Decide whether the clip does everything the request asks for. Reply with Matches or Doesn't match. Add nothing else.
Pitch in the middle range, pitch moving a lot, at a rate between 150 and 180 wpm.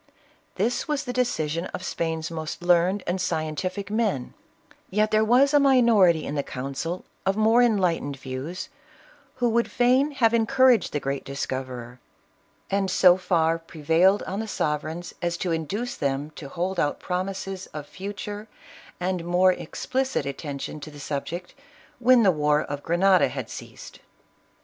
Matches